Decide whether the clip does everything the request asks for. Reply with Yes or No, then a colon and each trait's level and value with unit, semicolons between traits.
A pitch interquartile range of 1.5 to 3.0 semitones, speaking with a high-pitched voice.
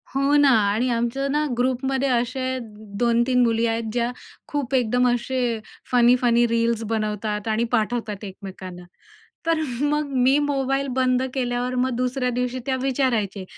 Yes: narrow, 2.4 semitones; high, 245 Hz